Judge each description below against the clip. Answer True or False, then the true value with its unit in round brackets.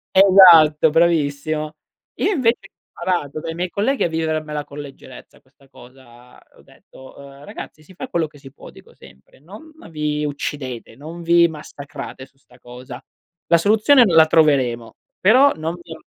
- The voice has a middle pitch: True (155 Hz)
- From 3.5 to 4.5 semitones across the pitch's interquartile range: True (3.8 semitones)